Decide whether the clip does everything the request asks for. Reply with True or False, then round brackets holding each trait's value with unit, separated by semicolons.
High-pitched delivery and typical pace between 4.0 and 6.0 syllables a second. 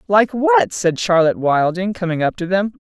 False (175 Hz; 5.0 syllables/s)